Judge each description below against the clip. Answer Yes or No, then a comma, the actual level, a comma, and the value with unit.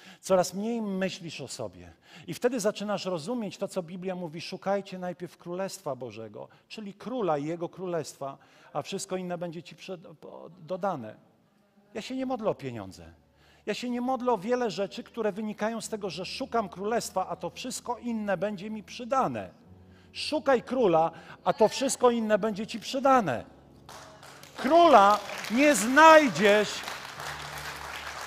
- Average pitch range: Yes, average, 4.8 semitones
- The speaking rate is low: No, average, 145 wpm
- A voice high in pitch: Yes, high, 195 Hz